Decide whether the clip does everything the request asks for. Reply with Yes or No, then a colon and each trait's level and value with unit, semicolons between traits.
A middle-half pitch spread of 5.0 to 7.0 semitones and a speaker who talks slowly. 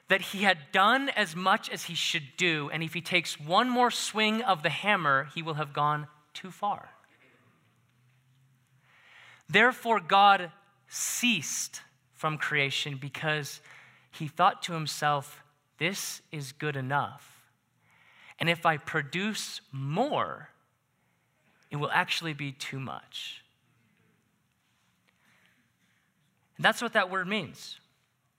Yes: average, 5.3 semitones; slow, 120 wpm